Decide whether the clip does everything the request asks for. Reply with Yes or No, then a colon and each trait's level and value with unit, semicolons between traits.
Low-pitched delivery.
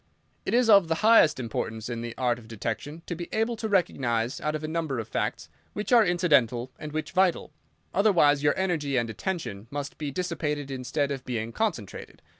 No: medium, 150 Hz